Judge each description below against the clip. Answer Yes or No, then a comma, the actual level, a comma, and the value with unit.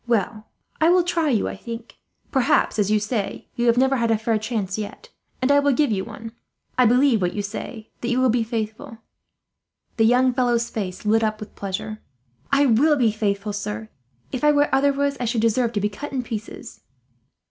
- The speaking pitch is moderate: No, high, 230 Hz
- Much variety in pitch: No, average, 3.4 semitones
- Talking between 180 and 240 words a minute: Yes, fast, 205 wpm